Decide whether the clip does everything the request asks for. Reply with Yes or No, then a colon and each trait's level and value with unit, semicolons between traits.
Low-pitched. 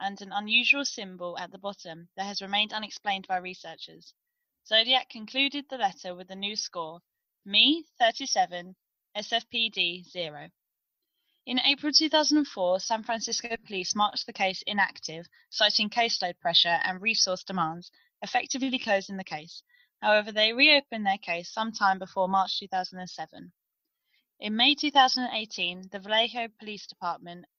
No: high, 210 Hz